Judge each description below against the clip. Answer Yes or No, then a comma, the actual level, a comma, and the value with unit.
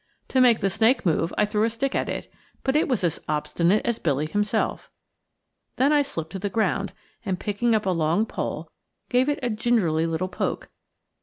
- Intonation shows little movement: No, wide, 5.6 semitones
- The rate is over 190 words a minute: Yes, average, 200 wpm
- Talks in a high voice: Yes, high, 210 Hz